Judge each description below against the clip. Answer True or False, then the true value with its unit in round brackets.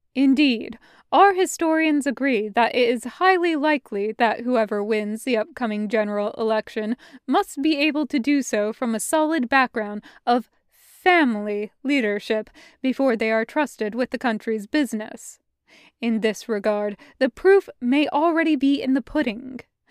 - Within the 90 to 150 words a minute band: True (145 wpm)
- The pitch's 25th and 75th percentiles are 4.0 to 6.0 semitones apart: True (5.1 semitones)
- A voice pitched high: True (250 Hz)